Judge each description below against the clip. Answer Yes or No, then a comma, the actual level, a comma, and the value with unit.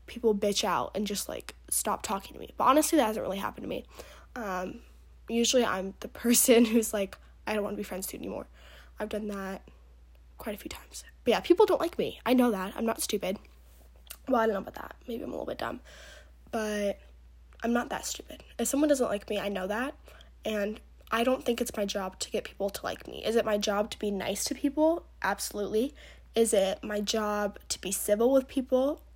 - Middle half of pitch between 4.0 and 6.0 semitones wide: No, average, 3.3 semitones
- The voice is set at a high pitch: Yes, high, 210 Hz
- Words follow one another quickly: Yes, fast, 225 wpm